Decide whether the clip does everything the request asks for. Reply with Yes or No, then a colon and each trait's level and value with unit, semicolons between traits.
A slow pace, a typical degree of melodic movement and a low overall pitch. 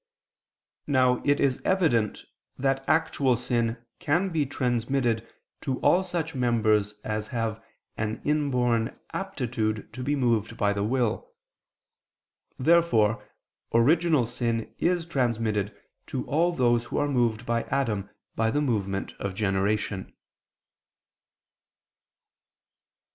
Yes: slow, 110 wpm; average, 4.5 semitones; low, 120 Hz